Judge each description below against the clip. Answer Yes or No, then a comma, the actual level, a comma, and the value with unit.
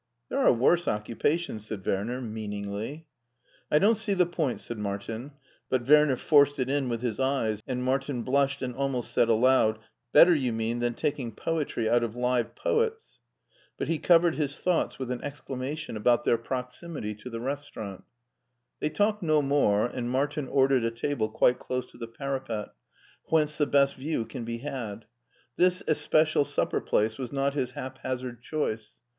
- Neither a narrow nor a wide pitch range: Yes, average, 4.1 semitones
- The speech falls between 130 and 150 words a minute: No, average, 175 wpm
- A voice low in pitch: Yes, low, 130 Hz